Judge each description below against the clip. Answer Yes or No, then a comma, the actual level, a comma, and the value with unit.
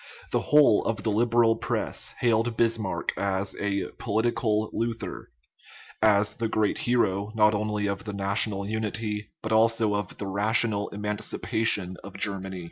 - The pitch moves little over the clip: Yes, narrow, 1.9 semitones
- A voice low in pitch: Yes, low, 105 Hz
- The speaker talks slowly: No, average, 150 wpm